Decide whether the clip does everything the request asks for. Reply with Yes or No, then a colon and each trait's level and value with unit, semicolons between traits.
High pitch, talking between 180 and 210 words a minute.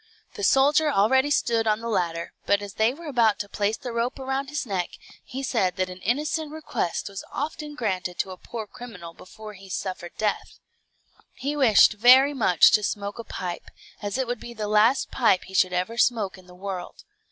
Yes: high, 220 Hz; average, 200 wpm